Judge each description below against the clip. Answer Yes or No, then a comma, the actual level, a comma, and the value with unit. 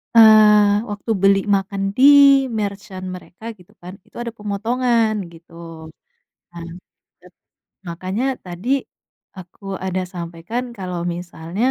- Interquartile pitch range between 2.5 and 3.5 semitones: No, average, 4.0 semitones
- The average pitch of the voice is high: Yes, high, 200 Hz